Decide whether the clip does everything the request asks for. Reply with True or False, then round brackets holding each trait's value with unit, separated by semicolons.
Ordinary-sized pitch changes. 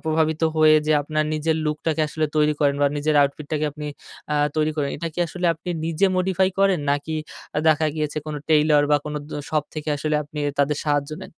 False (1.1 semitones)